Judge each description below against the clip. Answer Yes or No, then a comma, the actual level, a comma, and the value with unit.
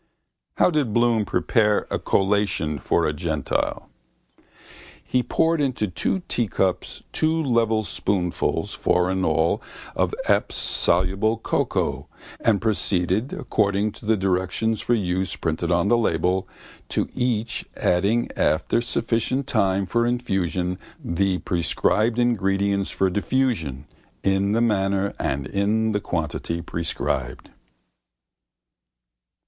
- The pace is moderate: No, slow, 115 wpm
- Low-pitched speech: Yes, low, 100 Hz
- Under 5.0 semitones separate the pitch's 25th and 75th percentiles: Yes, average, 4.2 semitones